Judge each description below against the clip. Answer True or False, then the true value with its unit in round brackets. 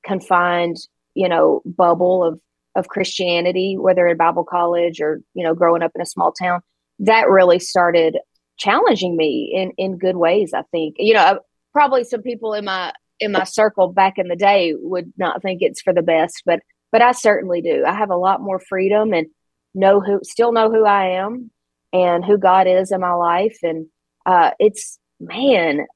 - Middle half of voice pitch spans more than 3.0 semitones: False (2.7 semitones)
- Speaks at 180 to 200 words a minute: True (190 wpm)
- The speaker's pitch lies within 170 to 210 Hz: True (185 Hz)